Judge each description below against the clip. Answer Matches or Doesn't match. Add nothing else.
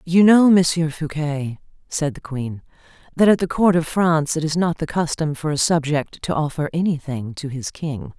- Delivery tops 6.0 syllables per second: Doesn't match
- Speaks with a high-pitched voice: Doesn't match